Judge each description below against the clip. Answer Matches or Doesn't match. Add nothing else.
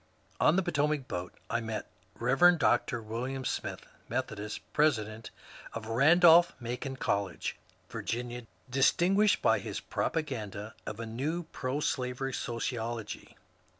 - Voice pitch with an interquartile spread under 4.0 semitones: Doesn't match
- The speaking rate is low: Matches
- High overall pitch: Doesn't match